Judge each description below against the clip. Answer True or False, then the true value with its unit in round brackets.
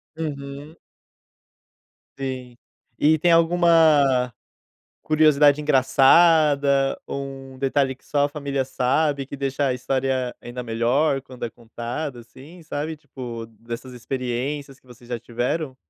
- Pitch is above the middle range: False (135 Hz)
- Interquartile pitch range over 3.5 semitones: False (3.1 semitones)